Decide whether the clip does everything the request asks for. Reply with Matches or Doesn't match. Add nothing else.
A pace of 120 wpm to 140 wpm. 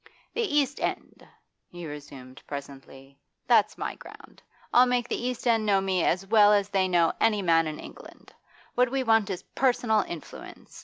Doesn't match